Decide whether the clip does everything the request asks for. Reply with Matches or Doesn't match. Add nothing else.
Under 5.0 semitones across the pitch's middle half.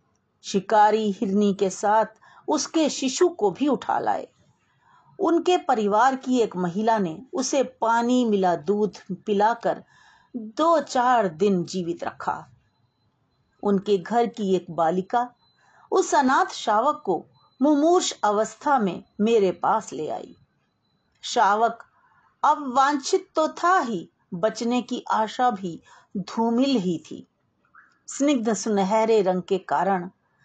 Doesn't match